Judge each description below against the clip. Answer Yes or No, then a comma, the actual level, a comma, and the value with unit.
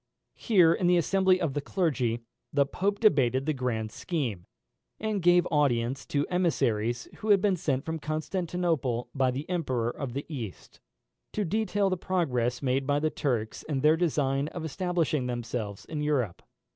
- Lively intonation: Yes, wide, 5.9 semitones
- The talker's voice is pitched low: No, medium, 150 Hz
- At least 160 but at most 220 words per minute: Yes, average, 165 wpm